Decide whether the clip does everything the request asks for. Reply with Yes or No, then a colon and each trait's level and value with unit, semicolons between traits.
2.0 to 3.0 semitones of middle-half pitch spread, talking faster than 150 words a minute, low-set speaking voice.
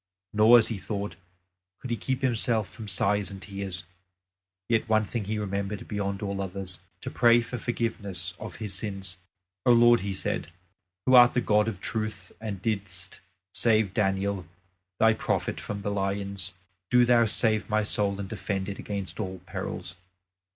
Yes: narrow, 2.4 semitones; average, 165 wpm; low, 105 Hz